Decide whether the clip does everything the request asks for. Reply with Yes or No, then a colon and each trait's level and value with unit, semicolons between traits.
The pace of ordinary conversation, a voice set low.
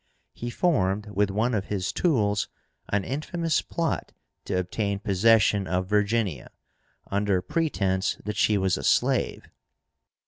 No: slow, 130 wpm; low, 105 Hz